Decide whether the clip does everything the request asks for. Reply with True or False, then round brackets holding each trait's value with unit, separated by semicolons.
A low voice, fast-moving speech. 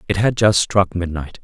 True (95 Hz; 210 wpm)